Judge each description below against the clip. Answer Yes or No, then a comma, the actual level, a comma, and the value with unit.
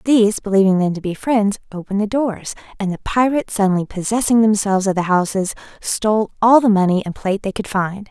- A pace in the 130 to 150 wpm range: No, average, 200 wpm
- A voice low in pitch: No, high, 205 Hz